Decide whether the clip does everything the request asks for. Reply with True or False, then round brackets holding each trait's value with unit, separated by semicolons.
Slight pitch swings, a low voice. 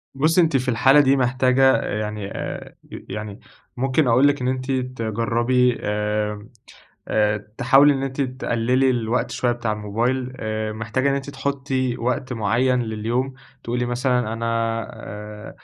False (3.2 semitones; 125 Hz)